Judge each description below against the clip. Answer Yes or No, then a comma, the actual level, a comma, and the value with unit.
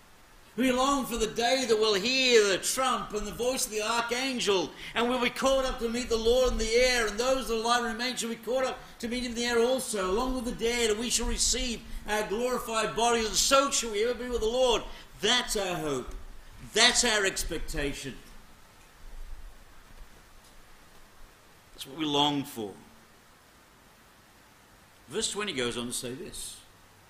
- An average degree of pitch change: No, wide, 7.9 semitones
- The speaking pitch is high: Yes, high, 225 Hz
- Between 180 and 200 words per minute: Yes, average, 190 wpm